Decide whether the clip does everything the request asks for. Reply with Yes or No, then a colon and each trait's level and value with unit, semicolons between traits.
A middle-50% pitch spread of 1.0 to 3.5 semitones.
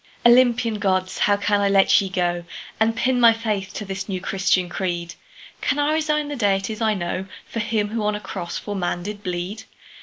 Yes: average, 3.2 semitones